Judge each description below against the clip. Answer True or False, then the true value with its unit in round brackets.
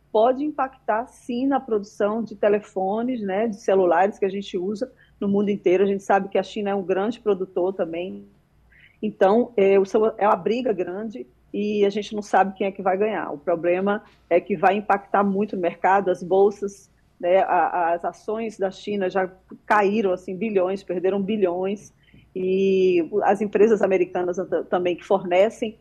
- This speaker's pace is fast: False (165 wpm)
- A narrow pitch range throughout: True (2.2 semitones)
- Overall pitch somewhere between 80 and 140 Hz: False (200 Hz)